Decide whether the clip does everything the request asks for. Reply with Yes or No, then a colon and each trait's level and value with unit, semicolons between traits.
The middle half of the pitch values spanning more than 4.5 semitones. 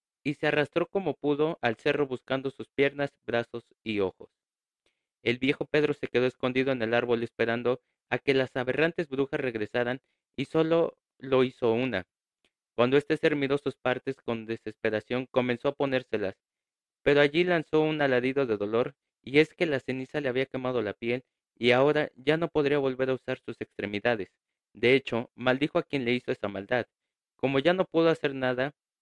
No: average, 3.2 semitones